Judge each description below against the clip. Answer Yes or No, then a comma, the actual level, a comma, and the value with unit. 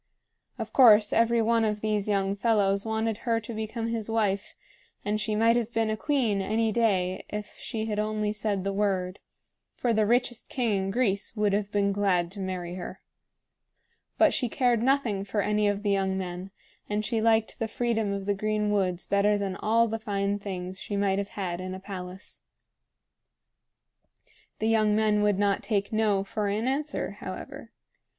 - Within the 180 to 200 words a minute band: Yes, average, 185 wpm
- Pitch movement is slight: Yes, narrow, 2.1 semitones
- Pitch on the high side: Yes, high, 210 Hz